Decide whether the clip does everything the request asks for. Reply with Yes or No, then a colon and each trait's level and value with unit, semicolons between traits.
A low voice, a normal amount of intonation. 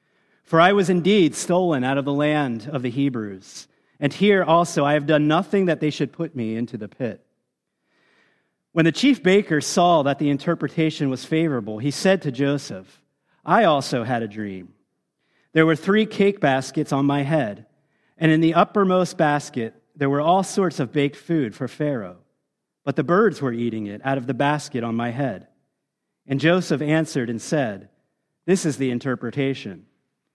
No: medium, 150 Hz; average, 4.1 semitones